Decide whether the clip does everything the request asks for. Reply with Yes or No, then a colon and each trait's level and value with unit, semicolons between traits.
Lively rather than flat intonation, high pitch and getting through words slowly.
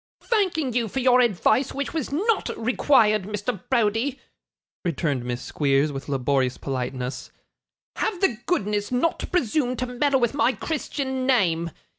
No: wide, 8.4 semitones; high, 240 Hz; average, 145 wpm